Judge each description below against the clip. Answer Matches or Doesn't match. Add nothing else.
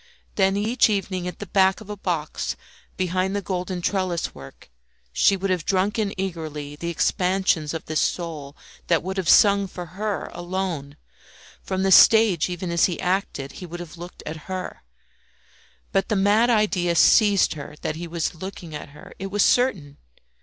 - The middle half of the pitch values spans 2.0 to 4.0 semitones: Matches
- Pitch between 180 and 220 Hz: Matches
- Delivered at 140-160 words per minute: Doesn't match